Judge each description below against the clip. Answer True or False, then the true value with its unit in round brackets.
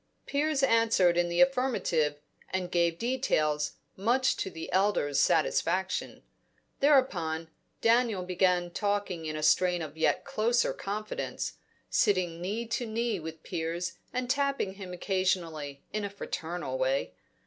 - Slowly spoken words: True (130 wpm)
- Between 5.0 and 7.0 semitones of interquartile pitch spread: True (5.6 semitones)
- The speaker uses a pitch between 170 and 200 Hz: True (185 Hz)